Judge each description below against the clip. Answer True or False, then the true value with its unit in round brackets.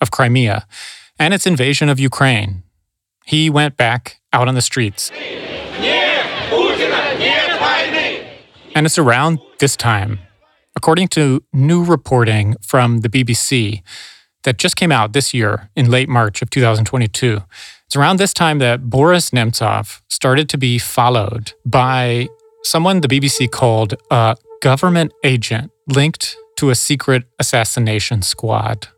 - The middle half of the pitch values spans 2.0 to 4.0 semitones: False (4.6 semitones)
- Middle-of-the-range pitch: False (125 Hz)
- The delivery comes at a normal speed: False (130 wpm)